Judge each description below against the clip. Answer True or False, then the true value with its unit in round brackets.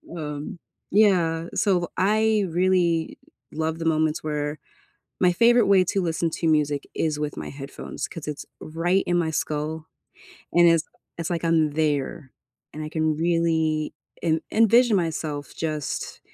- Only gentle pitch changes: True (2.3 semitones)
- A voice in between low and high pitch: True (165 Hz)